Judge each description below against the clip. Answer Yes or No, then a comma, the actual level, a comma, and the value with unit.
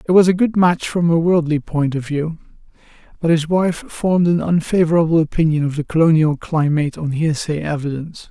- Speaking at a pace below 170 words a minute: No, average, 180 wpm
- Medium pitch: Yes, medium, 160 Hz